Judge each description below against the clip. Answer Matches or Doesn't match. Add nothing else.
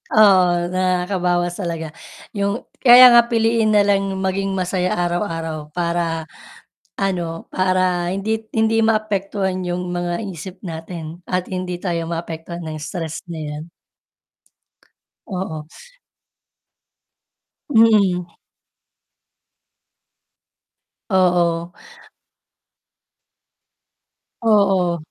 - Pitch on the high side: Doesn't match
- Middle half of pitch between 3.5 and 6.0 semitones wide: Doesn't match